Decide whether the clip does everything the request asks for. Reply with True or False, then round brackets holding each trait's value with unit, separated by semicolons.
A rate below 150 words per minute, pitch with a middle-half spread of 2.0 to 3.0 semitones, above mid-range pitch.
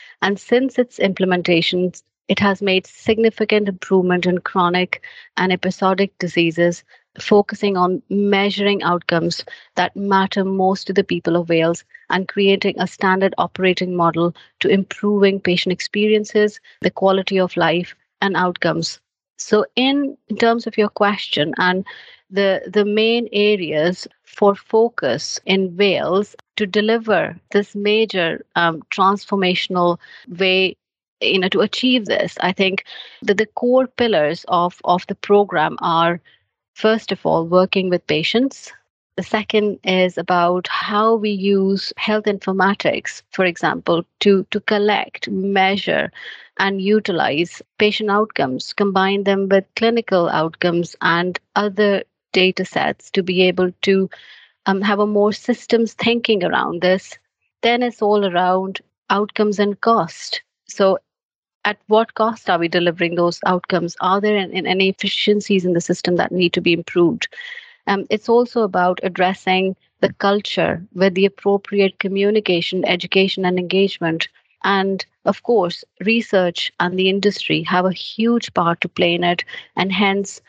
True (140 wpm; 2.5 semitones; 195 Hz)